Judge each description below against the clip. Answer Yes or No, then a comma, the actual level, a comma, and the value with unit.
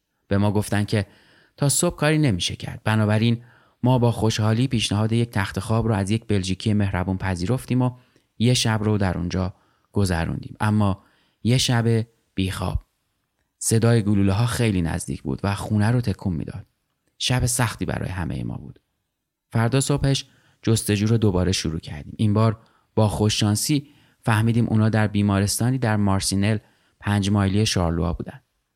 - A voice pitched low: Yes, low, 110 Hz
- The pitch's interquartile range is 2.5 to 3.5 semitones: Yes, average, 3.1 semitones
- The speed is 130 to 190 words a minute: Yes, average, 150 wpm